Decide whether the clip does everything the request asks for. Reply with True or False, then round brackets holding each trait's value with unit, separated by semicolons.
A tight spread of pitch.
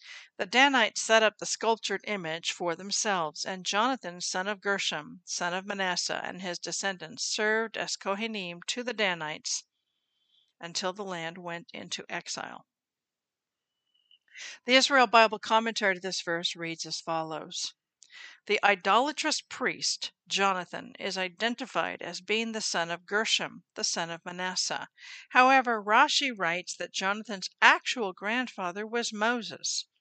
False (4.2 semitones)